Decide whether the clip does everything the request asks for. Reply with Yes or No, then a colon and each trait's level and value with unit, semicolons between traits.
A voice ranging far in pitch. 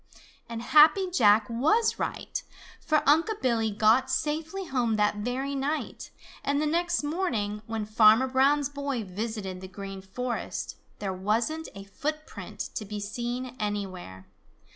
Yes: wide, 6.1 semitones